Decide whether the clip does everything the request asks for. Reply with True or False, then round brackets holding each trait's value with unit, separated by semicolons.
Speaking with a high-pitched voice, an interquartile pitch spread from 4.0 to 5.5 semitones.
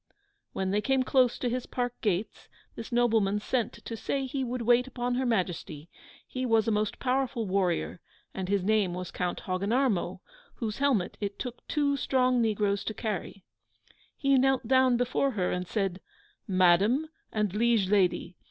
True (225 Hz; 4.6 semitones)